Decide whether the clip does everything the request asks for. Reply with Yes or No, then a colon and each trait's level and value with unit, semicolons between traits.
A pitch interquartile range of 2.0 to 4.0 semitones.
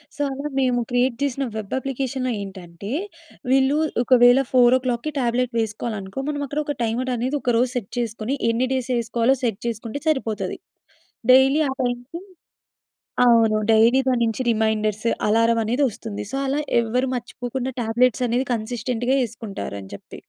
Yes: narrow, 2.6 semitones